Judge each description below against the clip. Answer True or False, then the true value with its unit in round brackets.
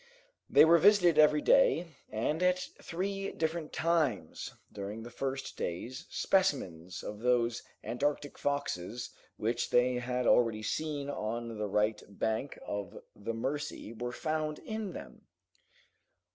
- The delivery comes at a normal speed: False (130 wpm)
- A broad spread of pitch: True (6.1 semitones)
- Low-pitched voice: True (130 Hz)